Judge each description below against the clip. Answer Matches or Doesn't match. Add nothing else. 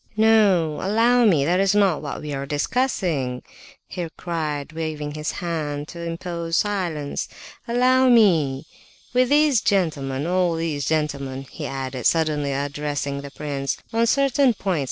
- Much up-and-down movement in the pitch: Matches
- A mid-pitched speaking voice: Matches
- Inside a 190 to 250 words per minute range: Doesn't match